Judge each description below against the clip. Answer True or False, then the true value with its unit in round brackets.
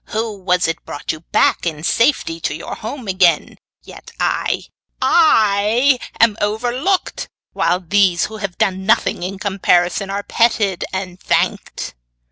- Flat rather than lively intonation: False (3.8 semitones)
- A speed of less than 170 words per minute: True (140 wpm)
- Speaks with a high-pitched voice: True (200 Hz)